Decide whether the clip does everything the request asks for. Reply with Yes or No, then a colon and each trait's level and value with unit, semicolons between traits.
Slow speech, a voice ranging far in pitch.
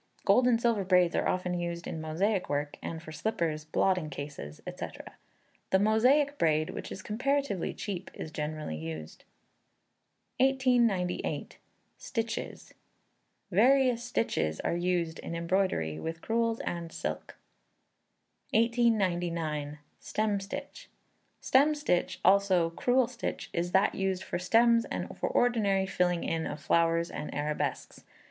Yes: slow, 125 wpm; wide, 5.9 semitones